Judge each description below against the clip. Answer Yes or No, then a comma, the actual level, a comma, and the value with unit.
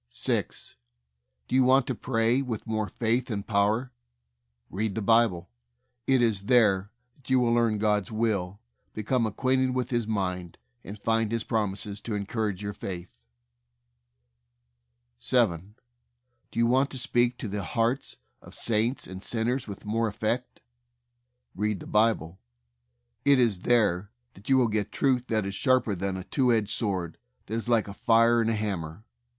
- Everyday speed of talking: Yes, average, 165 wpm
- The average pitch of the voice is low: Yes, low, 110 Hz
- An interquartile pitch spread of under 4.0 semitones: Yes, average, 3.1 semitones